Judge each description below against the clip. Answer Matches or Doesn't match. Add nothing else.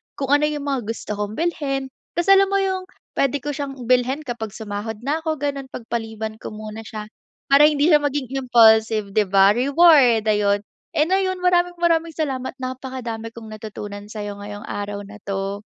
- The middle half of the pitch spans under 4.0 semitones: Doesn't match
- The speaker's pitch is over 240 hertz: Matches